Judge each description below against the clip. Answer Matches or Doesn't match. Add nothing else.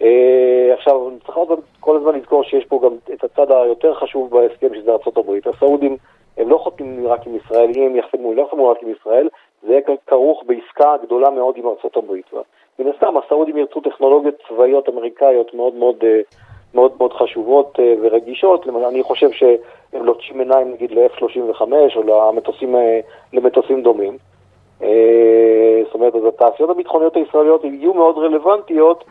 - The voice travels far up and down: Matches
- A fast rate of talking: Matches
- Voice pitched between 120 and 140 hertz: Matches